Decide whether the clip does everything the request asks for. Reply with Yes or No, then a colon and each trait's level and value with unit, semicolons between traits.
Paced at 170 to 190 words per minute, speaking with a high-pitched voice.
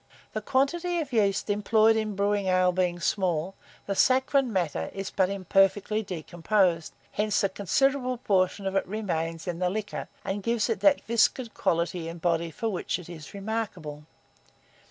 No: average, 160 wpm; high, 195 Hz